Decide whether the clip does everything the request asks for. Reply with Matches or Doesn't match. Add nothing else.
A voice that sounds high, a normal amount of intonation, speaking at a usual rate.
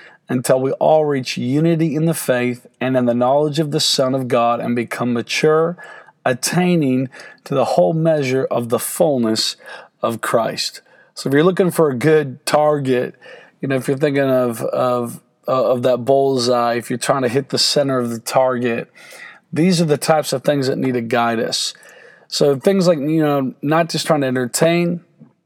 Doesn't match